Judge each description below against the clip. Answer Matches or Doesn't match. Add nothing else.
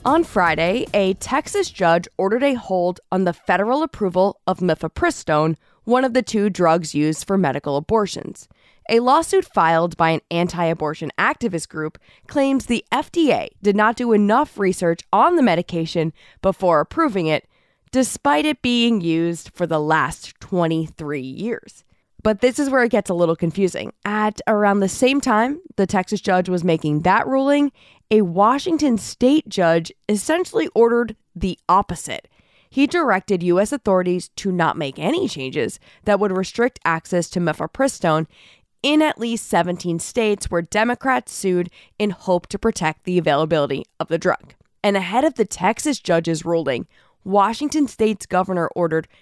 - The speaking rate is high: Doesn't match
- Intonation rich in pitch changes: Matches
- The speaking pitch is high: Matches